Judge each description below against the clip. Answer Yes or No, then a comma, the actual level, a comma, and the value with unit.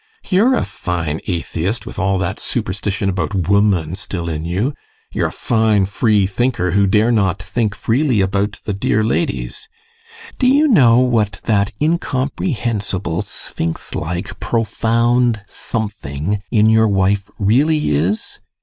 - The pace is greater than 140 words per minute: No, slow, 135 wpm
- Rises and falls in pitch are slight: No, average, 3.7 semitones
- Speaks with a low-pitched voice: Yes, low, 105 Hz